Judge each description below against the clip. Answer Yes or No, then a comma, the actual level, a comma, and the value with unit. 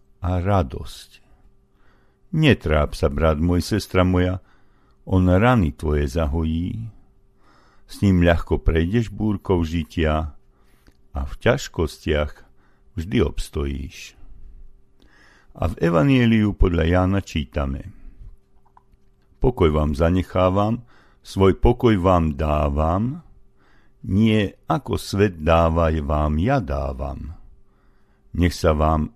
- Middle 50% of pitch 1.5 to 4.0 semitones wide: No, average, 4.4 semitones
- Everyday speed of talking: No, slow, 95 wpm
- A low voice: Yes, very low, 85 Hz